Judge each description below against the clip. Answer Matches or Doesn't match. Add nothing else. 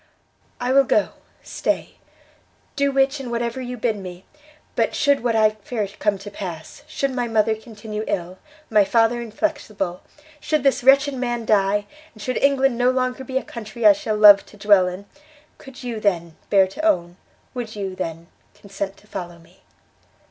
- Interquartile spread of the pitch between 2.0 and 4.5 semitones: Matches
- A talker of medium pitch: Doesn't match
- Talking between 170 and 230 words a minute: Matches